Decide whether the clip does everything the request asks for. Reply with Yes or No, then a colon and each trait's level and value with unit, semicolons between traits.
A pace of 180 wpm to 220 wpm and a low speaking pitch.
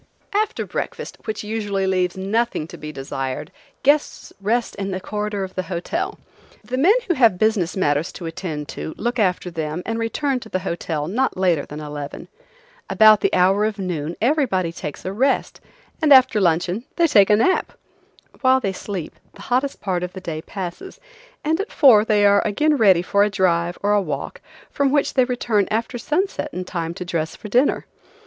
No: average, 190 wpm; high, 200 Hz